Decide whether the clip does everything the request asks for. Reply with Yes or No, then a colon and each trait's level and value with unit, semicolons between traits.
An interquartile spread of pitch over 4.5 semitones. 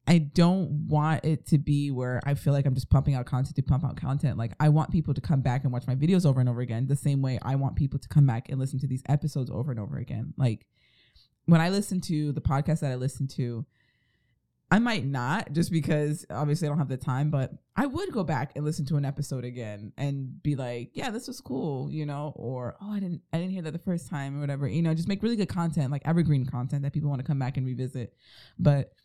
No: average, 3.4 semitones